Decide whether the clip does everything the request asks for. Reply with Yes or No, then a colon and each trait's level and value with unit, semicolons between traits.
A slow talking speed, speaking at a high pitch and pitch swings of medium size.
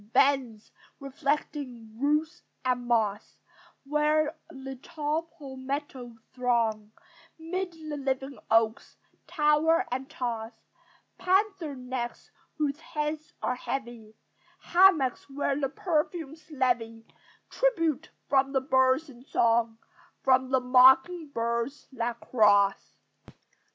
Yes: slow, 100 wpm; very high, 270 Hz; average, 4.1 semitones